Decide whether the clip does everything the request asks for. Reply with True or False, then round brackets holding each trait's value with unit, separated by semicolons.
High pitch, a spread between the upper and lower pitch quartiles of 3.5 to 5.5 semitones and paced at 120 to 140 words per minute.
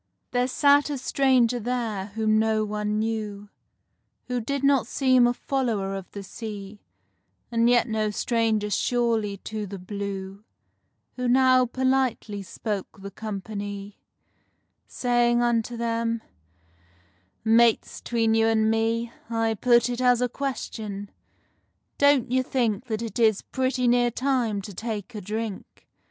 False (225 Hz; 2.8 semitones; 135 wpm)